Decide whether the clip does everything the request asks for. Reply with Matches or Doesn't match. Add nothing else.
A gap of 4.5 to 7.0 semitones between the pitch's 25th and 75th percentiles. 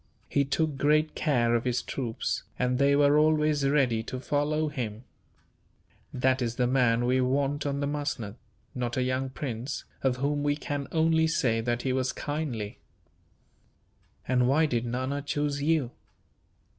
Doesn't match